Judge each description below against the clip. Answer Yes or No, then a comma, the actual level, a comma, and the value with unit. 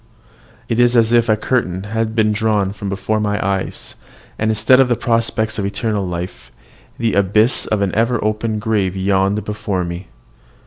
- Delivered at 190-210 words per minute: No, average, 170 wpm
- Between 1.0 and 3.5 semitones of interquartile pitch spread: Yes, narrow, 2.4 semitones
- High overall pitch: No, low, 105 Hz